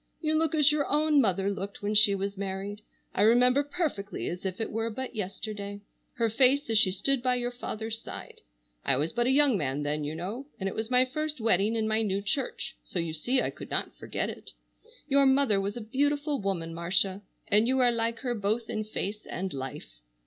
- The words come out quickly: Yes, fast, 215 wpm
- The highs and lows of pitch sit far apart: No, average, 4.8 semitones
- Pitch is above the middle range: Yes, high, 220 Hz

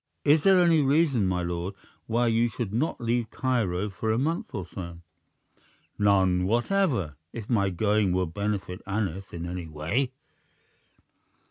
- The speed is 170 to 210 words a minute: No, average, 145 wpm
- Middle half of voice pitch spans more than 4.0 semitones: Yes, average, 5.1 semitones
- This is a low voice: Yes, low, 105 Hz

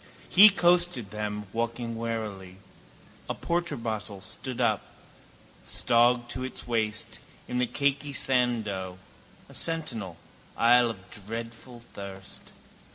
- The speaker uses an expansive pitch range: No, average, 3.3 semitones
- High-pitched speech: No, low, 115 Hz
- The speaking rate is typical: No, slow, 110 wpm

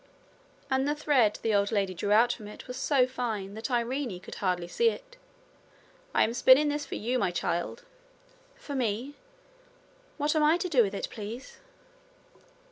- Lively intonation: Yes, wide, 5.7 semitones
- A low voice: No, high, 245 Hz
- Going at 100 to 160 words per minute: No, average, 175 wpm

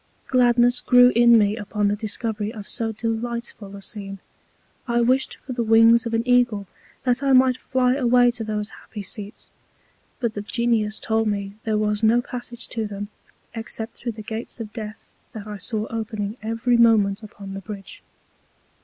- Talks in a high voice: Yes, high, 225 Hz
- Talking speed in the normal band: Yes, average, 175 wpm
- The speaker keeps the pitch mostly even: Yes, narrow, 2.3 semitones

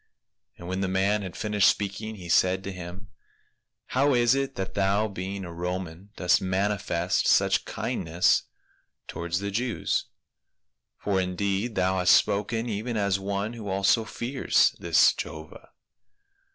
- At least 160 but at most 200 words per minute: No, average, 145 wpm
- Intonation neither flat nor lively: No, narrow, 2.3 semitones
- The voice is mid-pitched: No, low, 100 Hz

